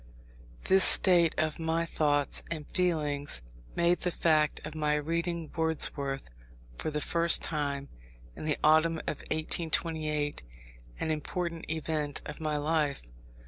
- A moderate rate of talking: No, slow, 130 wpm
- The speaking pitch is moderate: Yes, medium, 155 Hz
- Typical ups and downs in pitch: No, narrow, 1.9 semitones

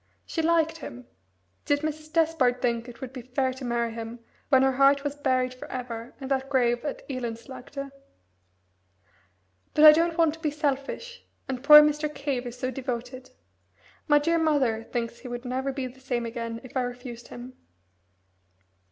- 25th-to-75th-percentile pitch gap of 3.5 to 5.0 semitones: No, average, 3.1 semitones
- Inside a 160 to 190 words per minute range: Yes, average, 175 wpm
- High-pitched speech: Yes, very high, 260 Hz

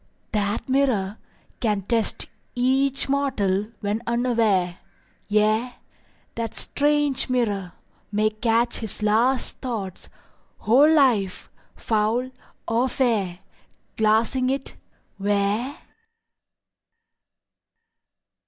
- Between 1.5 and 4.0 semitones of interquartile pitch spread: Yes, average, 3.7 semitones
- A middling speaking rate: No, slow, 80 wpm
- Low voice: No, high, 225 Hz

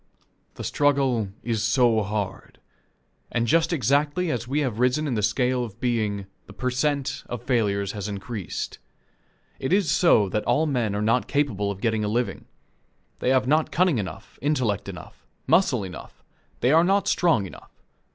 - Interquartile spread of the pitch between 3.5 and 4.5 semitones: No, average, 5.2 semitones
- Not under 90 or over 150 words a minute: No, average, 170 wpm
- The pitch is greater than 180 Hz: No, low, 120 Hz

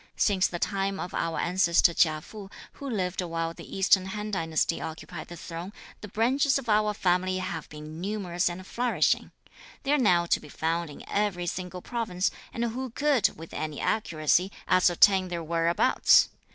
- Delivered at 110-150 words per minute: No, average, 170 wpm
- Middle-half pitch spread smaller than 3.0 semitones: No, average, 3.7 semitones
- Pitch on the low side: No, medium, 185 Hz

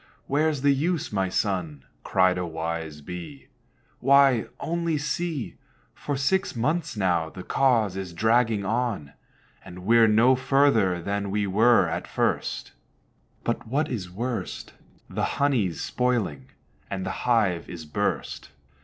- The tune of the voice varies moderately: No, wide, 6.9 semitones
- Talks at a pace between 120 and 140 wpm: Yes, slow, 135 wpm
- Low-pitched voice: Yes, low, 110 Hz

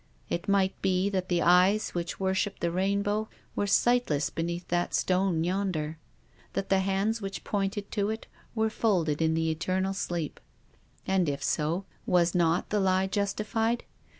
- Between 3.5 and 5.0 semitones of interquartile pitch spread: No, average, 2.8 semitones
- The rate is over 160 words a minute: Yes, average, 175 wpm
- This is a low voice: No, high, 190 Hz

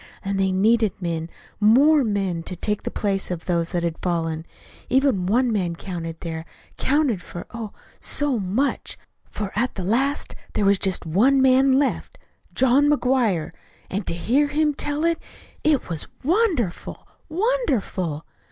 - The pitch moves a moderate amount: No, wide, 7.4 semitones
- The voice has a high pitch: Yes, high, 210 Hz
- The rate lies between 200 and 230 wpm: No, average, 150 wpm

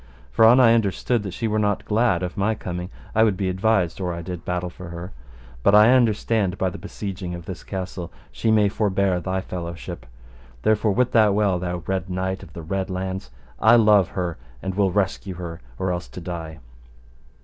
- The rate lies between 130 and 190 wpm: No, fast, 205 wpm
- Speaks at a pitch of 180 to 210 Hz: No, very low, 95 Hz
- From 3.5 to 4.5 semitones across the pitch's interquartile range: No, average, 2.9 semitones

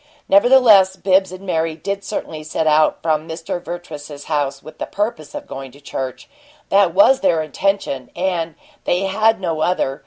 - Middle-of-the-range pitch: Yes, medium, 170 Hz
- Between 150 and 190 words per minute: Yes, average, 165 wpm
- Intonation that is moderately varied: Yes, average, 4.1 semitones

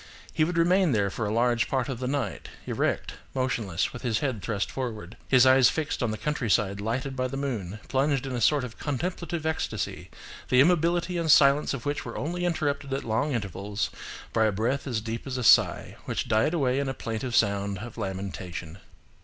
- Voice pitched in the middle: No, low, 125 Hz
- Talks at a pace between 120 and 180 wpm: No, average, 200 wpm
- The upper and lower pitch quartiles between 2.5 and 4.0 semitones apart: No, average, 4.7 semitones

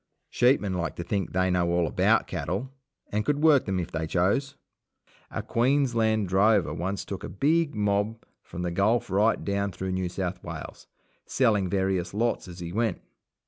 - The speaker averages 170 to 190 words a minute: Yes, average, 180 wpm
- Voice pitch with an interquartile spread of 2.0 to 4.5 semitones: Yes, average, 4.0 semitones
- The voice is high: No, low, 100 Hz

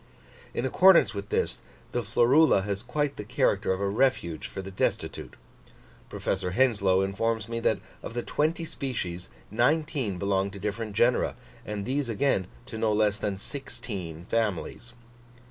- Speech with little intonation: No, average, 4.2 semitones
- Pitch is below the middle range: Yes, low, 110 Hz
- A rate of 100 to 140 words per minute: No, average, 150 wpm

